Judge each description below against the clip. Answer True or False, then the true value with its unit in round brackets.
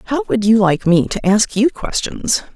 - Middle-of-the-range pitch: False (220 Hz)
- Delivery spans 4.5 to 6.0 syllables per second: False (4.2 syllables/s)